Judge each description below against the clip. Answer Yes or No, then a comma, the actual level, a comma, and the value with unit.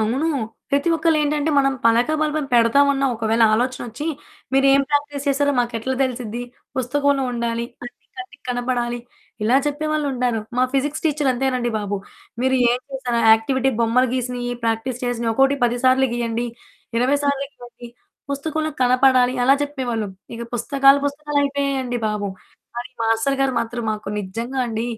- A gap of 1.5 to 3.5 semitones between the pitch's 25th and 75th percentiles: Yes, average, 2.9 semitones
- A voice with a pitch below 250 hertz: No, very high, 255 Hz